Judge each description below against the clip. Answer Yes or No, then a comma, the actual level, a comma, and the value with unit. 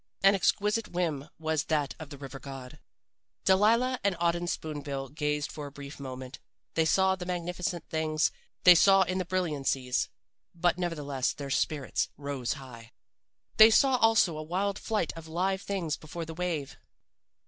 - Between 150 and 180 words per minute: Yes, average, 165 wpm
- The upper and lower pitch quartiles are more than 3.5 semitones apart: Yes, average, 4.5 semitones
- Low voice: No, medium, 160 Hz